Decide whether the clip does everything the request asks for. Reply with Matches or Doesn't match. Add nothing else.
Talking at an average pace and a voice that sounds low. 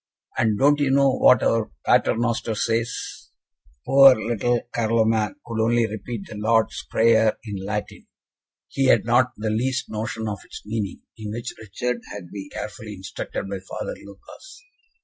Matches